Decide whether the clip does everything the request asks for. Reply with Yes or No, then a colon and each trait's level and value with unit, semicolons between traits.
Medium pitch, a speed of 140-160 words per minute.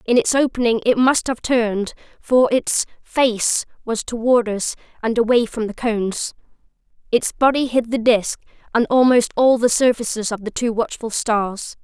No: high, 235 Hz; average, 155 wpm